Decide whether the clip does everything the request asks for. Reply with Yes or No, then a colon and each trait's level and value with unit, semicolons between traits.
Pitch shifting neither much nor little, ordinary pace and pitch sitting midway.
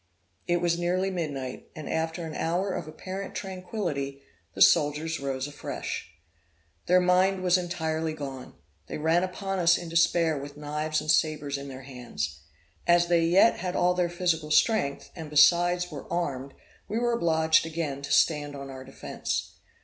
Yes: average, 3.3 semitones; average, 165 wpm; medium, 160 Hz